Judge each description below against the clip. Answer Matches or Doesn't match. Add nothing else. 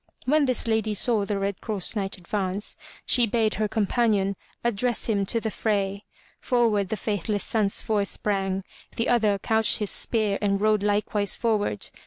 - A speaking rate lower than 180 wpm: Matches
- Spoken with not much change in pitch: Matches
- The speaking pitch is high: Matches